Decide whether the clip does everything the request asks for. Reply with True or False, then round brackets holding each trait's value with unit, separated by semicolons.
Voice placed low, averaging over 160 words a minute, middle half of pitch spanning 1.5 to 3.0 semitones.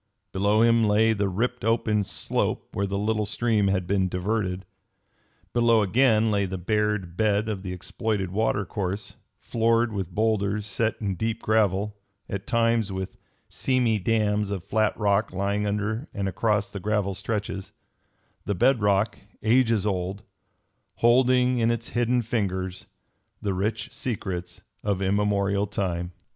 False (105 Hz; 145 wpm; 2.5 semitones)